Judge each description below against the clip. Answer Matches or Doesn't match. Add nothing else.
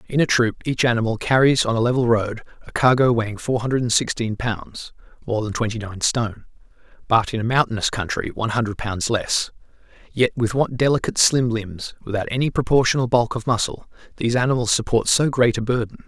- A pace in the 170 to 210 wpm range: Matches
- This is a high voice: Doesn't match